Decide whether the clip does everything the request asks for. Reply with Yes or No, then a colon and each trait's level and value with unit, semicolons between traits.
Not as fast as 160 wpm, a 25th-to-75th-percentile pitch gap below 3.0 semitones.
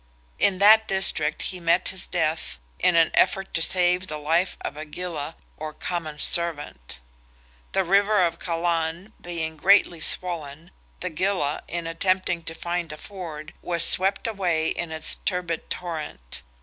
Yes: average, 150 wpm; narrow, 2.6 semitones